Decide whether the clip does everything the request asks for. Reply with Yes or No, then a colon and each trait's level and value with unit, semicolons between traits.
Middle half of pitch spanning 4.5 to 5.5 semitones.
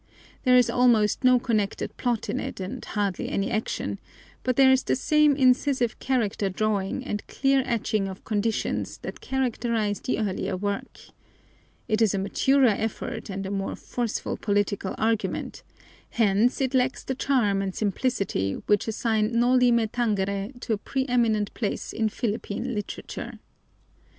No: average, 3.7 semitones